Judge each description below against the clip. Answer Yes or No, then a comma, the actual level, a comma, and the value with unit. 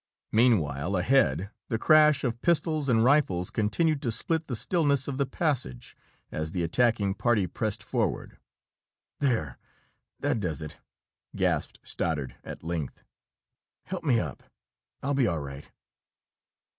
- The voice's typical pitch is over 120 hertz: No, low, 115 Hz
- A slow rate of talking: Yes, slow, 130 wpm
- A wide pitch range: Yes, wide, 8.7 semitones